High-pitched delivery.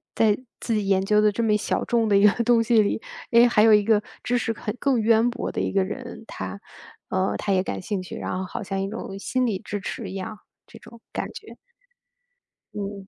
Yes: high, 210 Hz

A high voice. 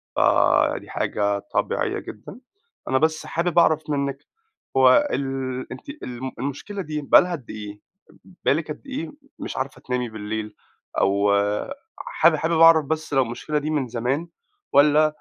No: medium, 140 Hz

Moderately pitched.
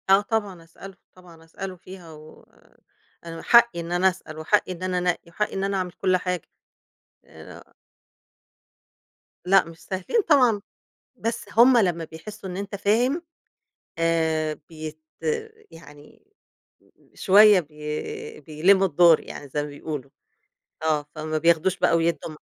Yes: medium, 180 Hz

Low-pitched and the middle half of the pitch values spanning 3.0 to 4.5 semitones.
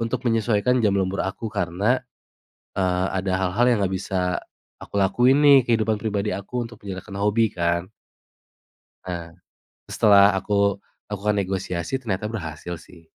Yes: low, 100 Hz; average, 3.4 semitones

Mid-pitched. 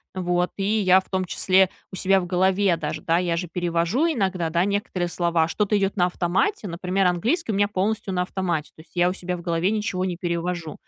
Yes: medium, 180 Hz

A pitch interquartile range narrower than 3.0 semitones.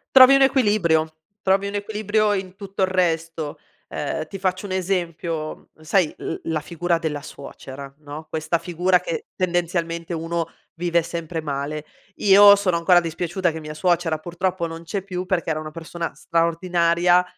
Yes: narrow, 2.6 semitones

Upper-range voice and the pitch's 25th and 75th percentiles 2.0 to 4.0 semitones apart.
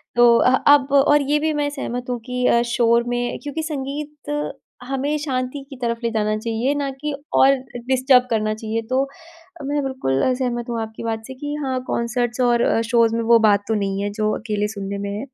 Yes: high, 245 Hz; average, 3.4 semitones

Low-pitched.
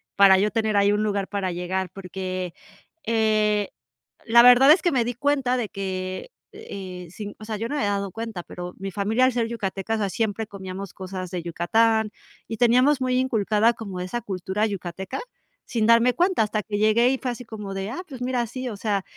No: high, 215 Hz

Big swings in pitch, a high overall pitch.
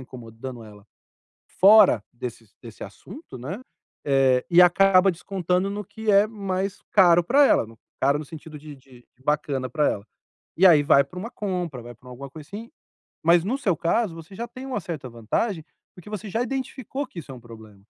No: wide, 7.3 semitones; medium, 170 Hz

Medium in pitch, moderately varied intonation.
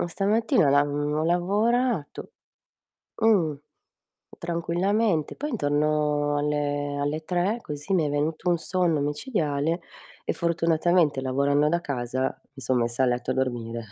Yes: medium, 150 Hz; average, 3.5 semitones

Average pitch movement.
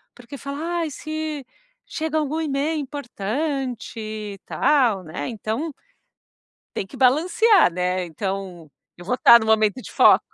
No: wide, 7.1 semitones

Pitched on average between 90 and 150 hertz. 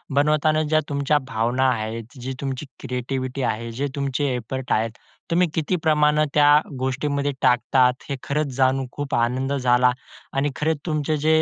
Yes: low, 135 Hz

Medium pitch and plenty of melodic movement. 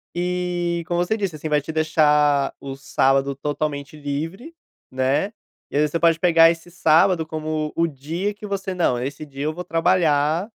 No: medium, 160 Hz; average, 3.2 semitones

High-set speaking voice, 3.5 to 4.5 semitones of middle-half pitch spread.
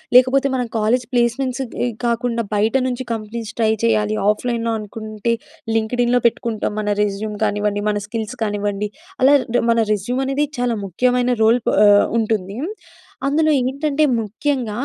No: high, 230 Hz; average, 2.8 semitones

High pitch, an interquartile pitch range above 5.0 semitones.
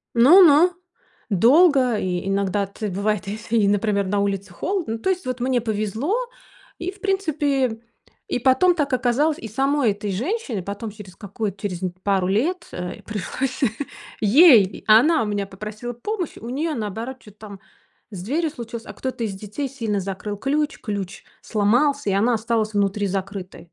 Yes: high, 225 Hz; wide, 5.4 semitones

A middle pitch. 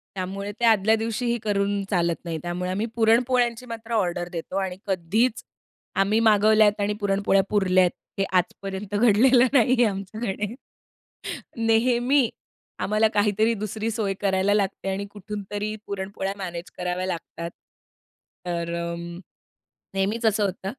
No: high, 205 Hz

